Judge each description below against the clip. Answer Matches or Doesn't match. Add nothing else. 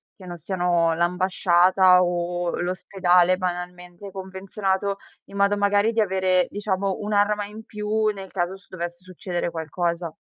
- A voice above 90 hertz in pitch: Matches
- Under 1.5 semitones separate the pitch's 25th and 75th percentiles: Doesn't match